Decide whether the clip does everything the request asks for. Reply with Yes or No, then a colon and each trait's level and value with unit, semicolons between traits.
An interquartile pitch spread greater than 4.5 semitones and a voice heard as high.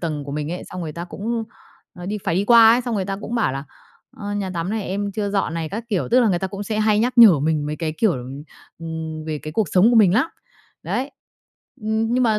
Yes: average, 5.1 semitones; high, 195 Hz